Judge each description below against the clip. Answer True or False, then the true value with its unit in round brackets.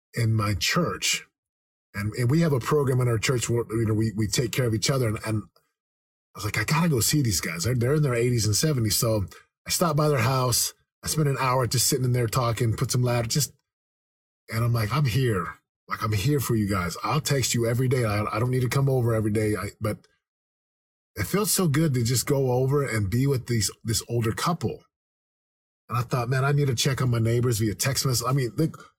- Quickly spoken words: True (245 wpm)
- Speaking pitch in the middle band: False (120 Hz)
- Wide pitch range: False (3.8 semitones)